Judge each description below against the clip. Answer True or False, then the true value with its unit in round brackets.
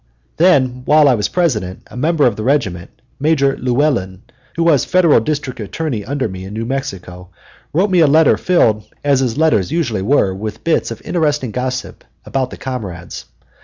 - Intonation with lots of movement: True (6.1 semitones)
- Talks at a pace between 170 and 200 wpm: True (175 wpm)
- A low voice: True (130 Hz)